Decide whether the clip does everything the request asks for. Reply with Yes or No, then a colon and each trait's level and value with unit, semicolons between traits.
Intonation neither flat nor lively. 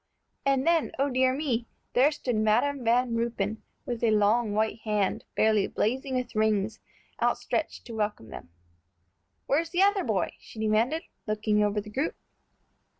Yes: average, 3.7 semitones